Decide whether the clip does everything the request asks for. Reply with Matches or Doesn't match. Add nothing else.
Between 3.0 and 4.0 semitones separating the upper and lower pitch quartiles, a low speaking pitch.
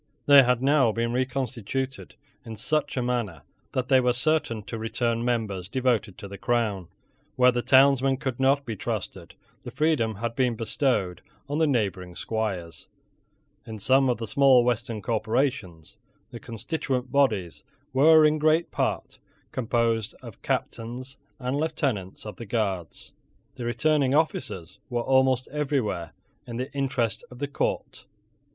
Matches